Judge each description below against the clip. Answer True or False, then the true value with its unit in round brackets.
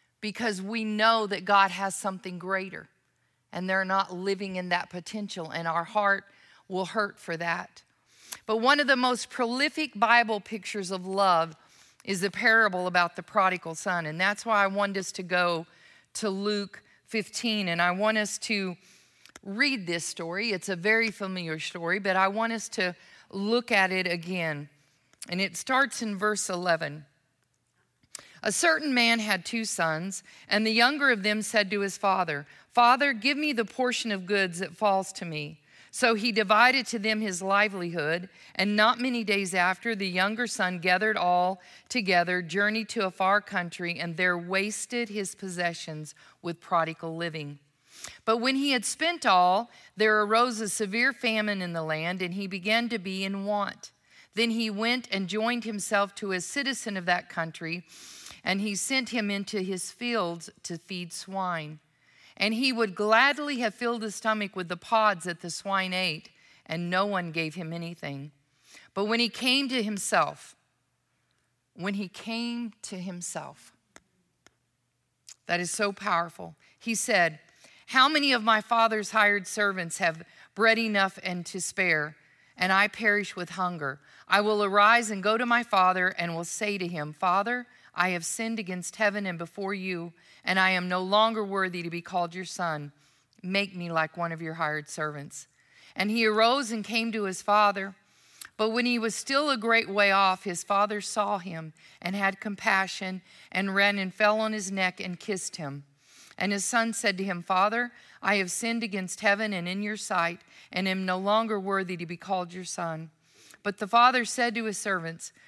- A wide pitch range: False (3.7 semitones)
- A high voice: True (195 Hz)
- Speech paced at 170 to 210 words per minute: True (180 wpm)